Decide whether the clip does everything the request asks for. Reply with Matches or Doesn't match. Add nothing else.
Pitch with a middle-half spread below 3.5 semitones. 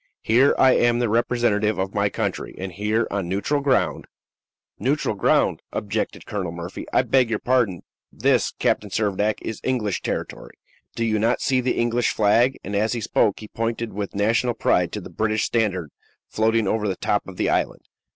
Matches